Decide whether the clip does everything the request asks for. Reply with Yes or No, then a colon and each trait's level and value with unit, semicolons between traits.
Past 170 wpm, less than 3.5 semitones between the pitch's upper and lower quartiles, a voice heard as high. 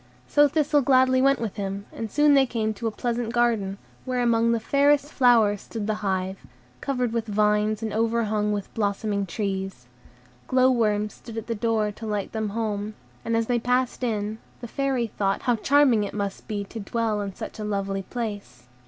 Yes: average, 190 wpm; average, 2.9 semitones; high, 220 Hz